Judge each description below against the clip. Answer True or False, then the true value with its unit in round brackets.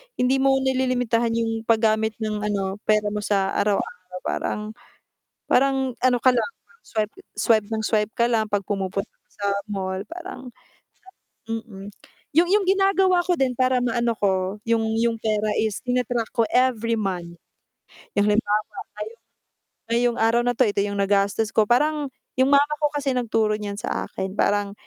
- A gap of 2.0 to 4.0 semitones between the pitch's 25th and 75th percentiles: True (3.5 semitones)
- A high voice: True (225 Hz)